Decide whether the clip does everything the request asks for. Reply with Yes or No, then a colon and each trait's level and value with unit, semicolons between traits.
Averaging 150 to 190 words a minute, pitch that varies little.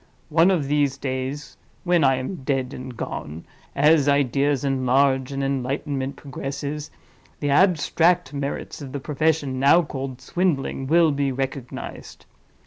No: slow, 135 wpm; narrow, 2.1 semitones